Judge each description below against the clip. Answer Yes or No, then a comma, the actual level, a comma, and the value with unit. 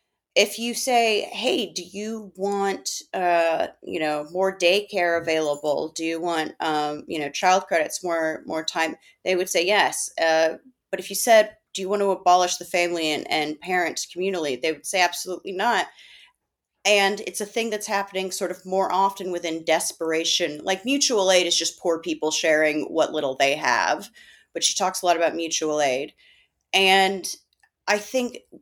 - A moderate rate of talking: Yes, average, 175 wpm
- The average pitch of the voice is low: No, medium, 180 Hz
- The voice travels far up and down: No, average, 3.3 semitones